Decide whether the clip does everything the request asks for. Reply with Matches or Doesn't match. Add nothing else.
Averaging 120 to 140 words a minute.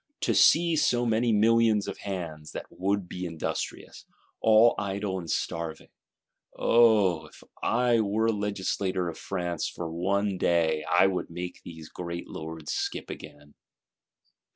Matches